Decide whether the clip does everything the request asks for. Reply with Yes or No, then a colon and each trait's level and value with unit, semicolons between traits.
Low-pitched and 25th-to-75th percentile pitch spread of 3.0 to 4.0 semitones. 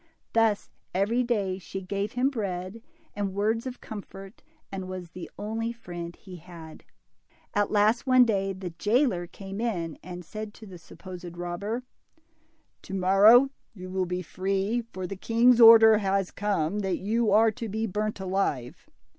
No: high, 200 Hz; average, 3.4 semitones